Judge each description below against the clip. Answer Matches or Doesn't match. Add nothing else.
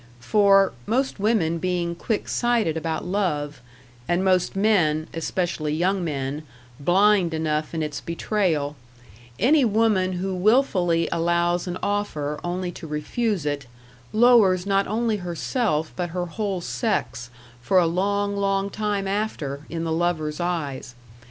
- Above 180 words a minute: Doesn't match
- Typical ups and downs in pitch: Matches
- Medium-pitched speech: Matches